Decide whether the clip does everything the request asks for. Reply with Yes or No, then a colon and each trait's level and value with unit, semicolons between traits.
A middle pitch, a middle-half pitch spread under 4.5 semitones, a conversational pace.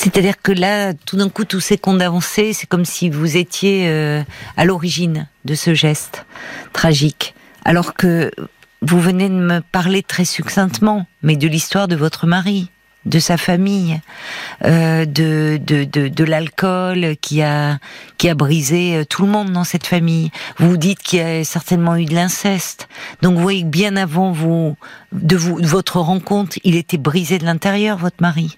Yes: medium, 175 Hz; average, 2.9 semitones; average, 180 wpm